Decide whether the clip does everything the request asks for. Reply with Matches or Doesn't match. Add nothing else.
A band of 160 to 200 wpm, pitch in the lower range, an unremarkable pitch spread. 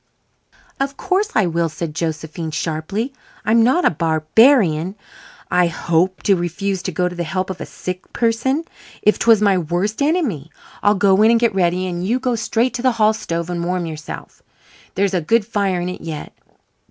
Doesn't match